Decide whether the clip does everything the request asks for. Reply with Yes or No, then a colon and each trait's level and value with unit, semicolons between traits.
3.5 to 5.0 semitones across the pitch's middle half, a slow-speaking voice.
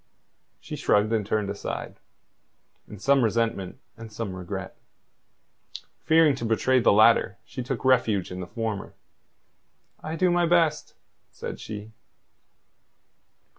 Yes: average, 4.5 semitones; slow, 125 wpm